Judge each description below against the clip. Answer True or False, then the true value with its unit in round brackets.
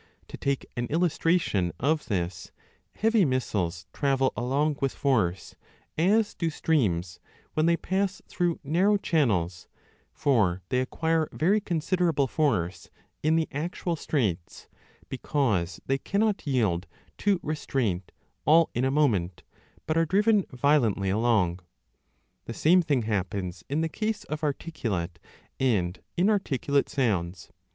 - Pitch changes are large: True (8.8 semitones)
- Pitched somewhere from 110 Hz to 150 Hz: True (140 Hz)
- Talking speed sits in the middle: False (130 wpm)